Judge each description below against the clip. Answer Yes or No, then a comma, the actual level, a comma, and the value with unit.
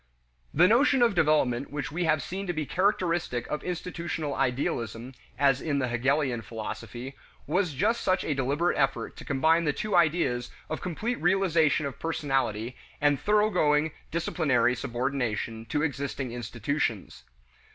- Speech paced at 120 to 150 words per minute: Yes, average, 140 wpm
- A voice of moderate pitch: Yes, medium, 145 Hz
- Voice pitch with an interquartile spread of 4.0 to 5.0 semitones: No, wide, 5.4 semitones